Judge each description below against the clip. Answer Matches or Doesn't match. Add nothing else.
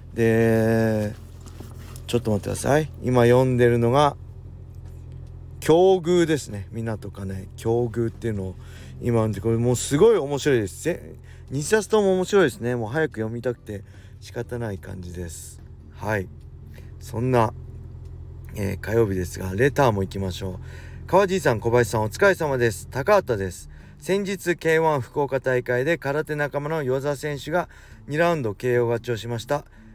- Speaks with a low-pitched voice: Matches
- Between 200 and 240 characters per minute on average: Doesn't match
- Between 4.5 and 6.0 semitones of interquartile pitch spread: Matches